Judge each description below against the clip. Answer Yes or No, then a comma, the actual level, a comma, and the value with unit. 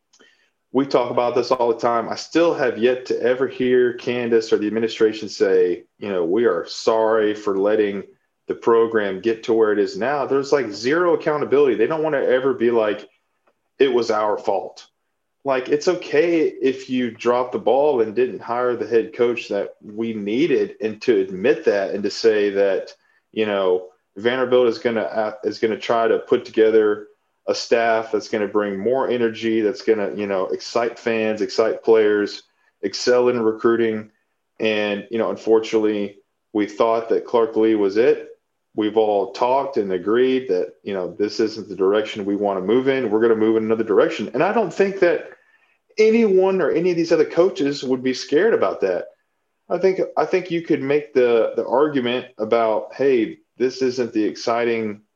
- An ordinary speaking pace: Yes, average, 190 wpm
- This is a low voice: Yes, low, 130 Hz